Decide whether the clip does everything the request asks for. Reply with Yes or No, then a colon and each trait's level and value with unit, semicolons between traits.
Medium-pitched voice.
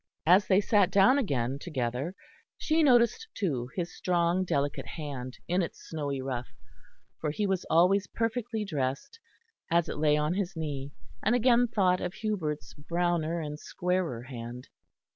Yes: medium, 170 Hz